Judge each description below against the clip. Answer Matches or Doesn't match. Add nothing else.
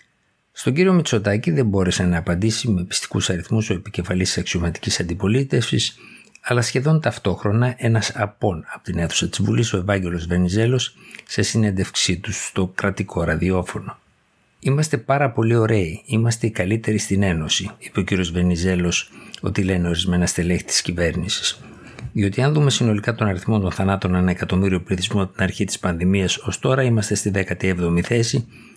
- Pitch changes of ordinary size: Matches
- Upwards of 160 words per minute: Doesn't match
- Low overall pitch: Matches